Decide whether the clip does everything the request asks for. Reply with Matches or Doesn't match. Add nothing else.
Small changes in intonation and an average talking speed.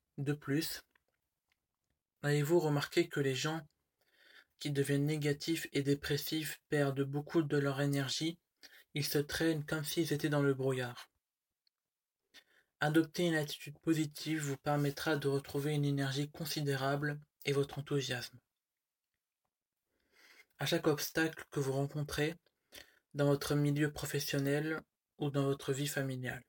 Doesn't match